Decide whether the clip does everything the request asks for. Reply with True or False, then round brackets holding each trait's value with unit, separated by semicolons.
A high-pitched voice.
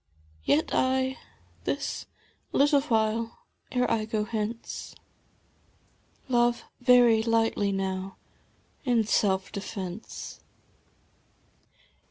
True (225 Hz)